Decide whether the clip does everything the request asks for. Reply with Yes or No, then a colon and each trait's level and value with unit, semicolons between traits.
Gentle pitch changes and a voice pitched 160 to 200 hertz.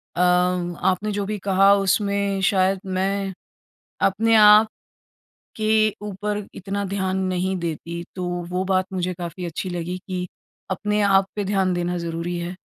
Yes: narrow, 1.9 semitones; high, 190 Hz